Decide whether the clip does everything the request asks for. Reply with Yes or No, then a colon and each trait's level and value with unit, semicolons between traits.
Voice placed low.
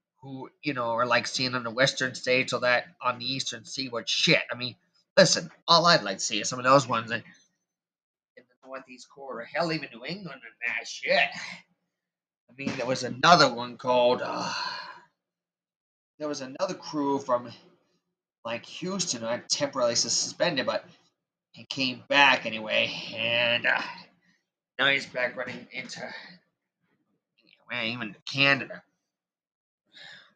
Yes: low, 130 Hz